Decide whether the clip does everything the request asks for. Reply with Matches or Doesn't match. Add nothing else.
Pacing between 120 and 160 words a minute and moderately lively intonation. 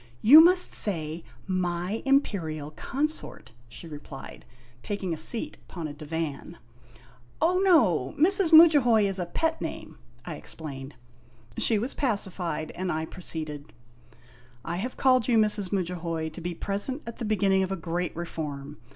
Doesn't match